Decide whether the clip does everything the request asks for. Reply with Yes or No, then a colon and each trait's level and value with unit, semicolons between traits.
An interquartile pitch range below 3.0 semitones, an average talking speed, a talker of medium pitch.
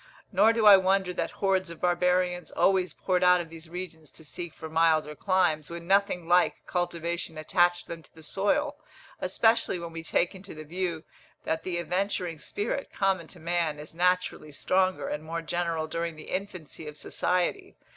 Yes: narrow, 2.4 semitones; average, 175 wpm; medium, 175 Hz